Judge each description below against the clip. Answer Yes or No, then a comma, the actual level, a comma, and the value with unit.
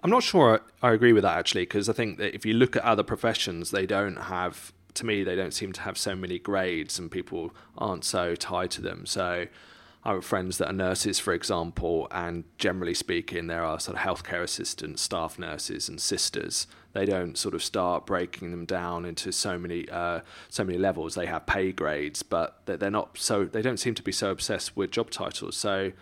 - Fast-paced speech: Yes, fast, 215 wpm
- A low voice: Yes, very low, 90 Hz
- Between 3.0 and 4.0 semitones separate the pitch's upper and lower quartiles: No, narrow, 2.6 semitones